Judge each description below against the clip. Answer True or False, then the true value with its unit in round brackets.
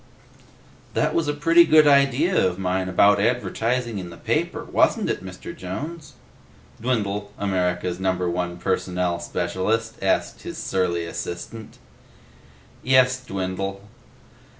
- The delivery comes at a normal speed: False (120 wpm)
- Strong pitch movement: True (5.8 semitones)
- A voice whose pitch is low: True (100 Hz)